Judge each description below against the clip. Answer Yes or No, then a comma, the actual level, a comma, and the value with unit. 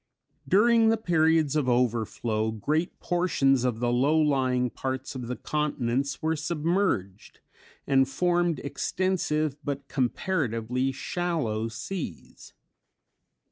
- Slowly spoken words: Yes, slow, 105 wpm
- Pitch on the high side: No, medium, 140 Hz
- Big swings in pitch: No, average, 5.0 semitones